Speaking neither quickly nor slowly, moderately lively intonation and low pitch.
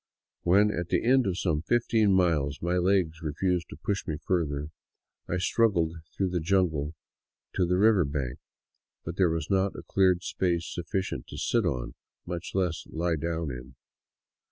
Yes: average, 170 wpm; average, 3.2 semitones; very low, 85 Hz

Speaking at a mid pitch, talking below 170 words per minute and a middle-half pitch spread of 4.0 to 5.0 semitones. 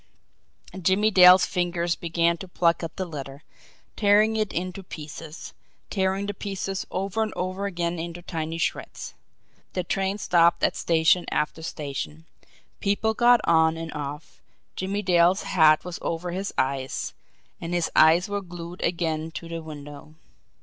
No: medium, 175 Hz; average, 150 wpm; average, 2.9 semitones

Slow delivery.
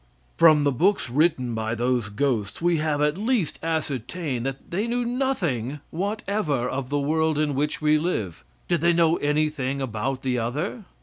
No: average, 170 wpm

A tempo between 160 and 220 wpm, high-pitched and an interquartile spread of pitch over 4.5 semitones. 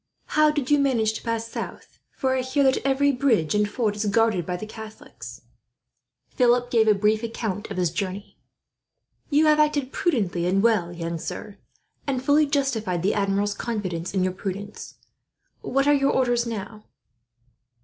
Yes: average, 170 wpm; high, 220 Hz; average, 4.9 semitones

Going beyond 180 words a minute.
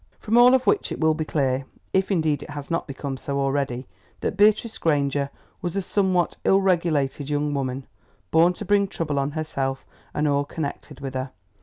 Yes: average, 190 wpm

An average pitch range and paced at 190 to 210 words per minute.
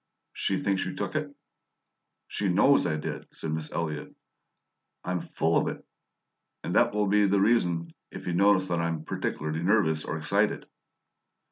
No: average, 3.9 semitones; average, 160 wpm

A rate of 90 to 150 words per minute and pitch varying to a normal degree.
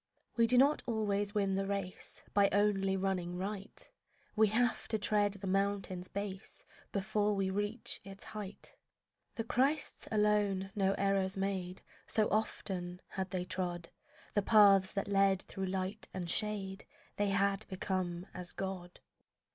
No: average, 145 wpm; narrow, 1.6 semitones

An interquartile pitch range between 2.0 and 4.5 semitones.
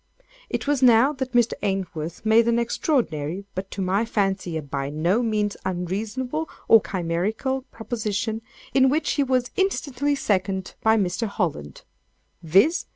No: average, 5.3 semitones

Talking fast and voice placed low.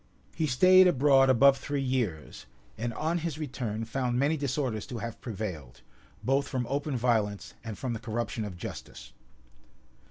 No: average, 155 wpm; low, 125 Hz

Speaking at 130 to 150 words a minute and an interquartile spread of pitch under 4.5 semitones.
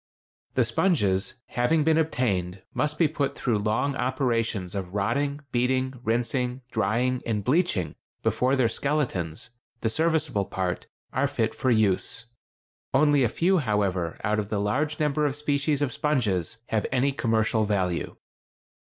No: slow, 135 wpm; average, 5.3 semitones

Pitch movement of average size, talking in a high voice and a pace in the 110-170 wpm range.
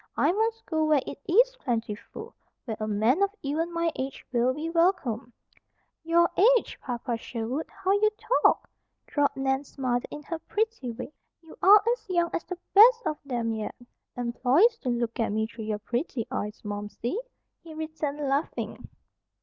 No: wide, 6.5 semitones; very high, 280 Hz; average, 165 wpm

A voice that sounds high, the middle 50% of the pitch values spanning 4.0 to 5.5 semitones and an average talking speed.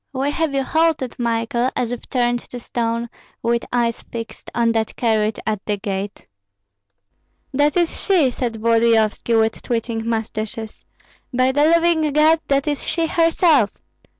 Yes: high, 240 Hz; average, 4.3 semitones; average, 150 wpm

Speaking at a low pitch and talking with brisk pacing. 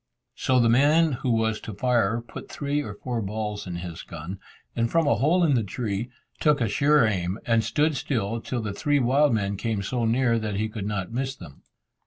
Yes: low, 115 Hz; fast, 215 wpm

